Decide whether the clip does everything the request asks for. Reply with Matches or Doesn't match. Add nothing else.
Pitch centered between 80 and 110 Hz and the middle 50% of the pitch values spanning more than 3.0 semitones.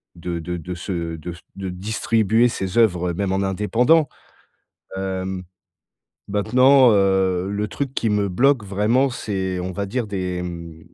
Matches